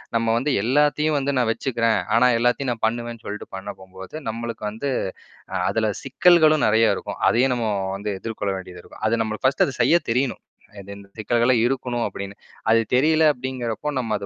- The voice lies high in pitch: No, low, 120 Hz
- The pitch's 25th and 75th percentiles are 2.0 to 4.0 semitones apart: Yes, average, 3.4 semitones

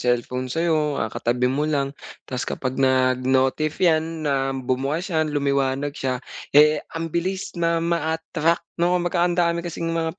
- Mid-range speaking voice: Yes, medium, 155 Hz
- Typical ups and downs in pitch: Yes, average, 4.0 semitones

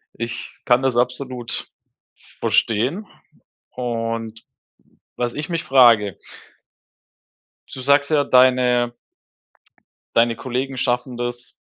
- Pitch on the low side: Yes, low, 125 Hz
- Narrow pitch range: Yes, narrow, 1.9 semitones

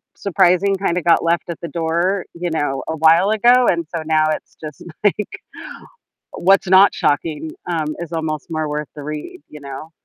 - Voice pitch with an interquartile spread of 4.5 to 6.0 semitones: No, average, 2.9 semitones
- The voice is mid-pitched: Yes, medium, 165 Hz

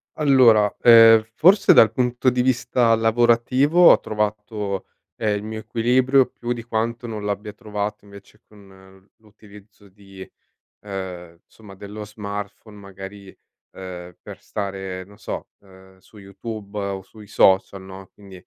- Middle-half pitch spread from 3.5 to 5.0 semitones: No, average, 2.7 semitones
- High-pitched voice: No, low, 105 Hz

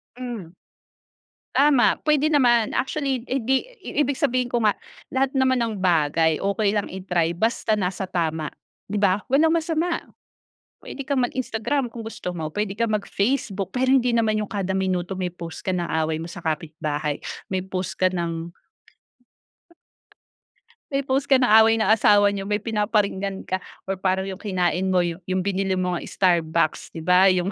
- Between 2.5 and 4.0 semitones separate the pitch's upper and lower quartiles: No, average, 5.0 semitones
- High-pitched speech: Yes, high, 200 Hz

